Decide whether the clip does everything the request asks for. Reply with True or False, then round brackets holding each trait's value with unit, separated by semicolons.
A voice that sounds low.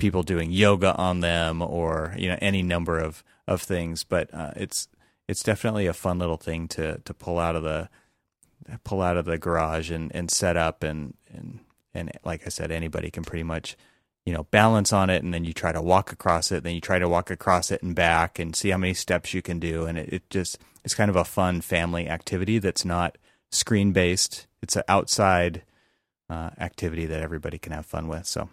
True (85 Hz)